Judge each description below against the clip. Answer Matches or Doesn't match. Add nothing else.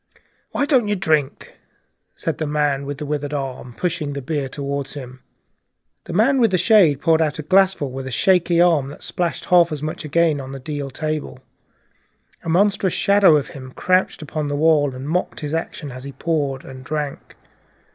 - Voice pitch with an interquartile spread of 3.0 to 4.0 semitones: Matches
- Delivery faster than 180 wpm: Matches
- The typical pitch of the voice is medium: Matches